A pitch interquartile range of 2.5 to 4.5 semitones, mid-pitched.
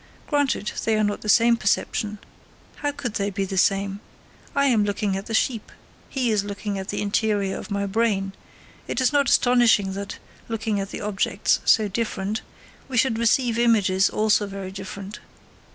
No: average, 2.8 semitones; high, 210 Hz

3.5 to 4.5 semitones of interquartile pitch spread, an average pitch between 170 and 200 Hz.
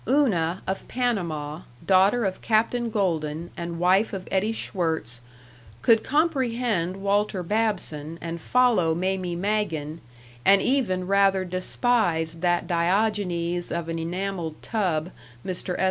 Yes: average, 4.1 semitones; medium, 185 Hz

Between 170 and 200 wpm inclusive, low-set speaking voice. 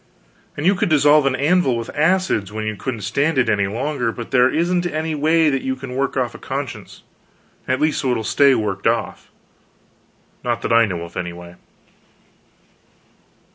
Yes: average, 180 wpm; low, 130 Hz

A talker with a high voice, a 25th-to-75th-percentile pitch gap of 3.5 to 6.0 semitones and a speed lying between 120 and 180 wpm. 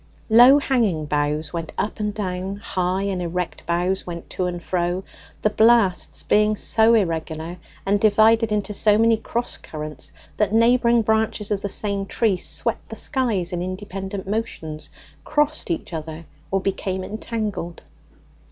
Yes: high, 195 Hz; average, 3.8 semitones; average, 150 wpm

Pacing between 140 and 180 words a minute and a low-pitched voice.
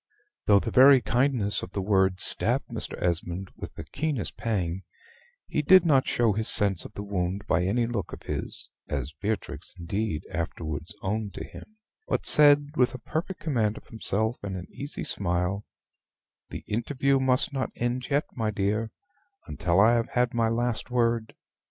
Yes: average, 170 wpm; low, 110 Hz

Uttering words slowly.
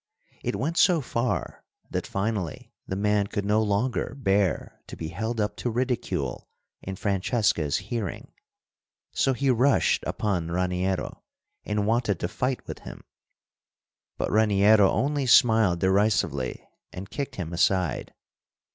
Yes: slow, 130 wpm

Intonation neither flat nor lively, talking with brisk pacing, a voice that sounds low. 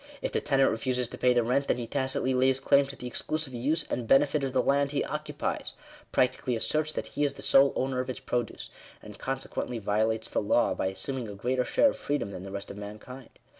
Yes: average, 3.2 semitones; fast, 240 wpm; low, 130 Hz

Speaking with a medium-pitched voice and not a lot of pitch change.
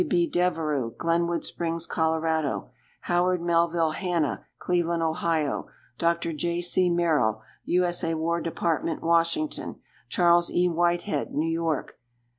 Yes: medium, 170 Hz; narrow, 1.3 semitones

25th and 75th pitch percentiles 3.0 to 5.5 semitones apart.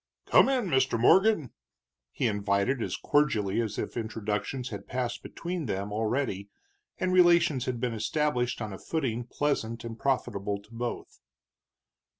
Yes: average, 4.9 semitones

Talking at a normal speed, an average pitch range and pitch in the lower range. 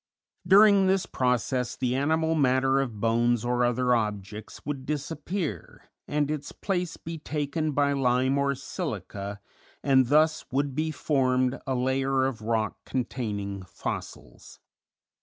No: slow, 130 wpm; average, 3.7 semitones; low, 130 Hz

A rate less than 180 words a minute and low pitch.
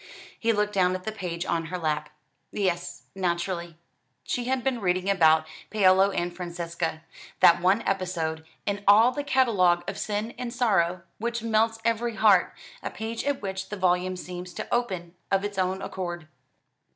No: average, 165 wpm; high, 190 Hz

